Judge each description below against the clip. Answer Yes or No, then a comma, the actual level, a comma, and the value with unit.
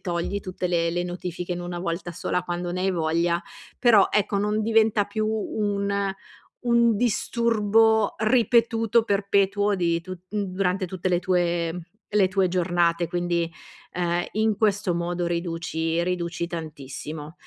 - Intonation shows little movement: No, average, 3.3 semitones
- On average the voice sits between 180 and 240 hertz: Yes, medium, 185 Hz